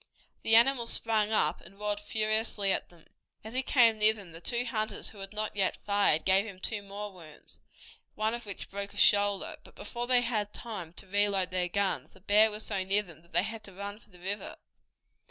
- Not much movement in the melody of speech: Yes, narrow, 2.1 semitones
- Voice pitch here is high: Yes, high, 205 Hz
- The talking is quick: Yes, fast, 220 wpm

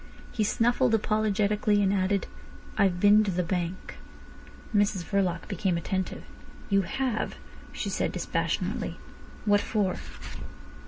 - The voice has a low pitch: No, high, 200 Hz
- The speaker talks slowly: Yes, slow, 115 wpm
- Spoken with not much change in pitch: Yes, narrow, 2.3 semitones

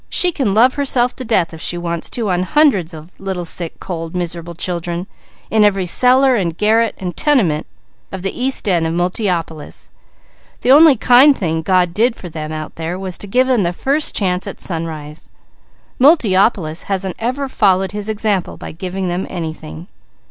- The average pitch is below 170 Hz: No, medium, 185 Hz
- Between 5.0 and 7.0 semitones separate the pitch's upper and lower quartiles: Yes, wide, 5.5 semitones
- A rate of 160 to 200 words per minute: Yes, average, 175 wpm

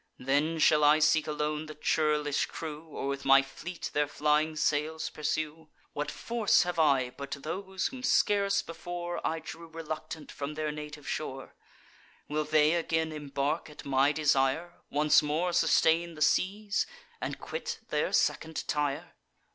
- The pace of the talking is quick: No, average, 150 wpm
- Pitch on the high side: No, medium, 155 Hz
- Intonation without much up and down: Yes, narrow, 2.0 semitones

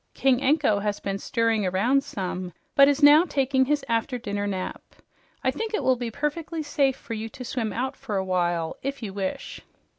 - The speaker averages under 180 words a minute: No, average, 200 wpm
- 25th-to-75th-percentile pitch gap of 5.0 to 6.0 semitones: Yes, wide, 5.5 semitones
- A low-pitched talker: No, high, 245 Hz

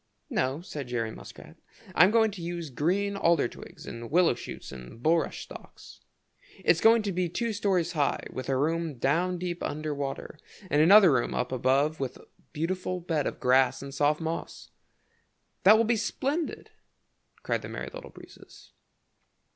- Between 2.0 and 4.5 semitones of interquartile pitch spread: No, average, 5.0 semitones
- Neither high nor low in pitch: Yes, medium, 165 Hz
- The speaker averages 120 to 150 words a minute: No, average, 165 wpm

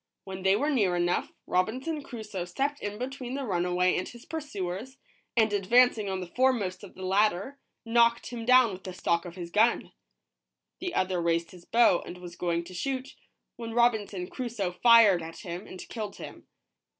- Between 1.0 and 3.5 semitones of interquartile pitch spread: No, average, 5.0 semitones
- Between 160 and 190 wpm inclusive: Yes, average, 185 wpm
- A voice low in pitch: No, high, 205 Hz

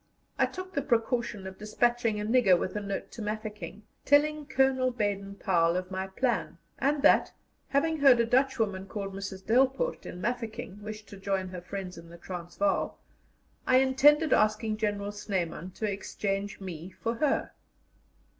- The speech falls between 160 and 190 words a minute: Yes, average, 165 wpm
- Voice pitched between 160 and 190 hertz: No, high, 210 Hz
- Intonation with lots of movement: No, average, 5.0 semitones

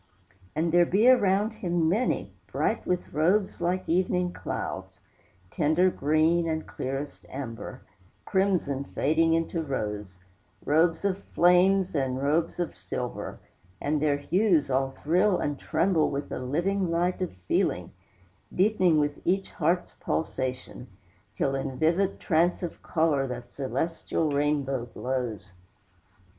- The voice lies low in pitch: No, medium, 160 Hz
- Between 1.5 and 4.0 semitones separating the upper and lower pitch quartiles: No, average, 4.6 semitones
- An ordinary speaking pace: No, slow, 125 wpm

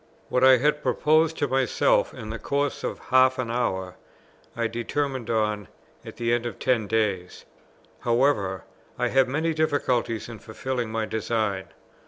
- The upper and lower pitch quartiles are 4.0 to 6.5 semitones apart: No, average, 3.4 semitones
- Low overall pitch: Yes, low, 120 Hz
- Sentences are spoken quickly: No, average, 155 wpm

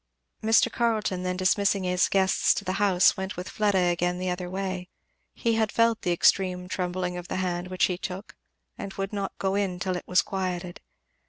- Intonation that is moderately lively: No, narrow, 1.7 semitones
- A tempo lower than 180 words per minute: No, average, 195 wpm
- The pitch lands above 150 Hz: Yes, medium, 185 Hz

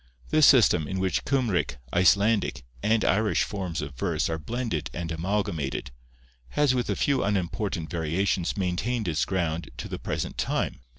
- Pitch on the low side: Yes, very low, 95 Hz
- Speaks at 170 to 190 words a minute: No, average, 155 wpm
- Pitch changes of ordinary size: Yes, average, 4.9 semitones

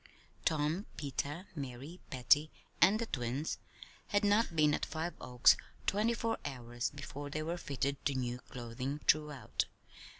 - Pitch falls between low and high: Yes, medium, 145 Hz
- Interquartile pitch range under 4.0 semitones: No, average, 4.6 semitones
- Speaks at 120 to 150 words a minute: Yes, average, 140 wpm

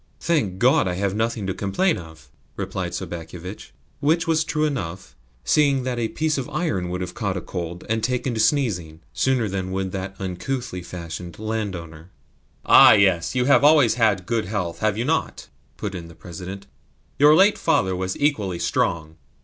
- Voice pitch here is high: No, low, 100 Hz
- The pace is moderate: Yes, average, 175 wpm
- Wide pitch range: Yes, wide, 6.5 semitones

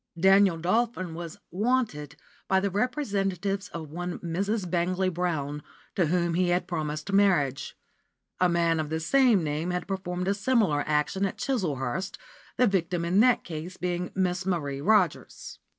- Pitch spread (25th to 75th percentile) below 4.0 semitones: Yes, average, 3.1 semitones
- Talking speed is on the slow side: No, average, 150 wpm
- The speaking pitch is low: No, medium, 180 Hz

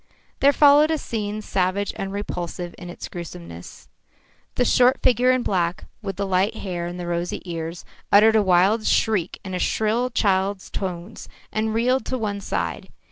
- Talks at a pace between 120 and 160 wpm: No, average, 170 wpm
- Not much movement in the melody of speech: No, average, 4.0 semitones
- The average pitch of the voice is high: Yes, high, 200 Hz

